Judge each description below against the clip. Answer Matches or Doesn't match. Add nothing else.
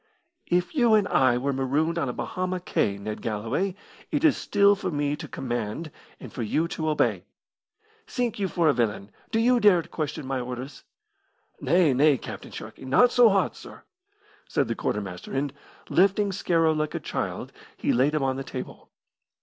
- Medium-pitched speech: Matches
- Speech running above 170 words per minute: Matches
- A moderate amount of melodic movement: Doesn't match